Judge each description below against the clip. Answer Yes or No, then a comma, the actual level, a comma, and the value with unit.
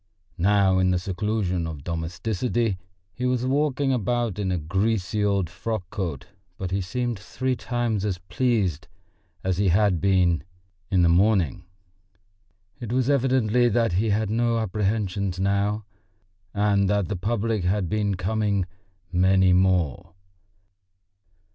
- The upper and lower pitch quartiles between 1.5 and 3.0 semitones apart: No, average, 3.6 semitones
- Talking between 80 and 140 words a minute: Yes, slow, 135 wpm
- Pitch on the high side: No, low, 100 Hz